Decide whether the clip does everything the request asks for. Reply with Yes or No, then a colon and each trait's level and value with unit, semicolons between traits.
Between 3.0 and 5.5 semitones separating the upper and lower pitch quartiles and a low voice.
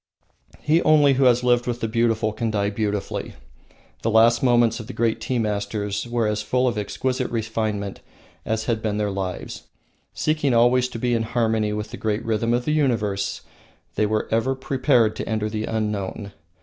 No: narrow, 2.4 semitones; low, 115 Hz